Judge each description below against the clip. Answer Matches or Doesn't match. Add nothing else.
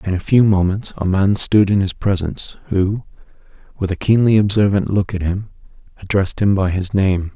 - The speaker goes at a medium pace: Matches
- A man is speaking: Matches